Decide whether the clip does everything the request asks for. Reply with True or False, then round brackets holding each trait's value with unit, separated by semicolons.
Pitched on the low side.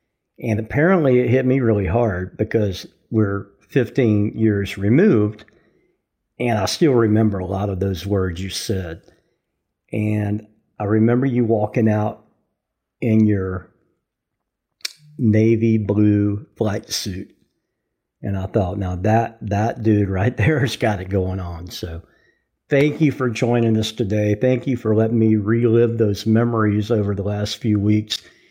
True (110 Hz)